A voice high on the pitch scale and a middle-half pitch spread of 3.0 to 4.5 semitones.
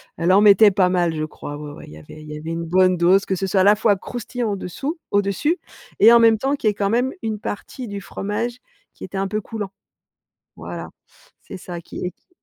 Yes: high, 195 Hz; average, 3.9 semitones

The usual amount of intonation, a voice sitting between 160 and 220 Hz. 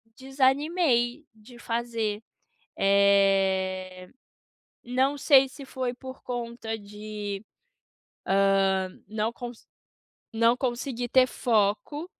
No: average, 4.2 semitones; high, 235 Hz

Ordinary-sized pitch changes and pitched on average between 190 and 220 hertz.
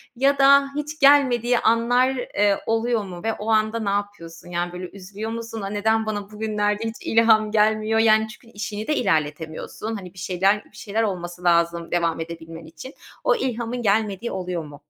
Yes: average, 4.0 semitones; high, 215 Hz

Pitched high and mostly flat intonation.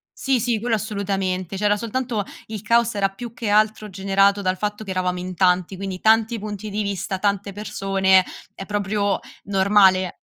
Yes: high, 200 Hz; narrow, 2.0 semitones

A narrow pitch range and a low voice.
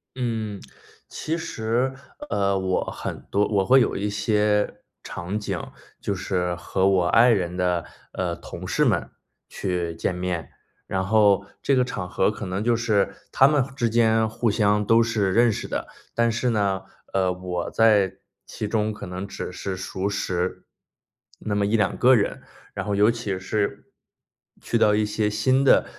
No: average, 3.0 semitones; low, 105 Hz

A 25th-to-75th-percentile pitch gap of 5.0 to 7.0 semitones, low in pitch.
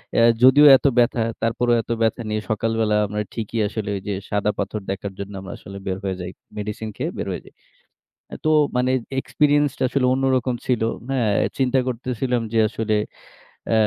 No: average, 3.4 semitones; low, 115 Hz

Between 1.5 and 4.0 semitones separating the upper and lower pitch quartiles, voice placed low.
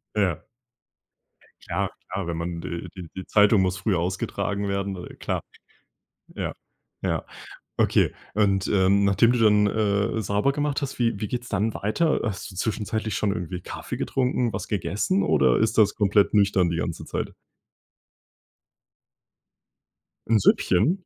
Yes: average, 2.7 semitones; low, 100 Hz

